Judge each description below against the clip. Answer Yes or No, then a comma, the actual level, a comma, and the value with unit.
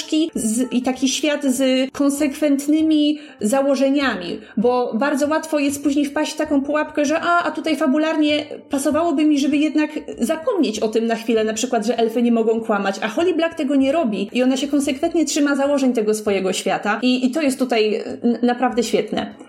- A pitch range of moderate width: Yes, average, 4.2 semitones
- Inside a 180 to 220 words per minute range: Yes, fast, 185 wpm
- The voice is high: Yes, very high, 275 Hz